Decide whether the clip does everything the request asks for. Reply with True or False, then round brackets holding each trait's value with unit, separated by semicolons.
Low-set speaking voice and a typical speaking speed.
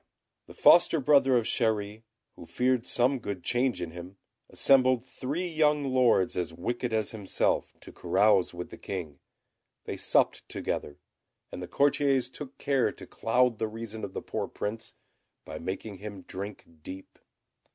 True (115 Hz; 155 wpm)